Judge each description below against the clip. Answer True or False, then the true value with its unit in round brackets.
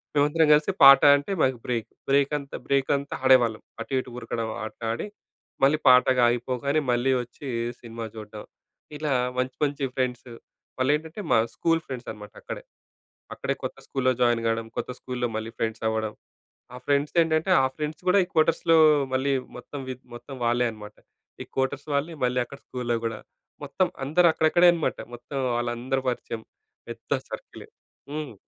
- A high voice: False (130 Hz)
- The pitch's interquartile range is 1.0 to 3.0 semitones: False (3.7 semitones)